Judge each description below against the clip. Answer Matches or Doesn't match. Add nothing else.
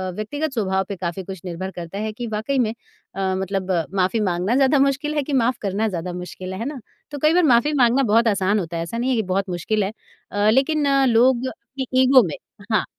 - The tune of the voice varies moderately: Doesn't match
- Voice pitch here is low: Doesn't match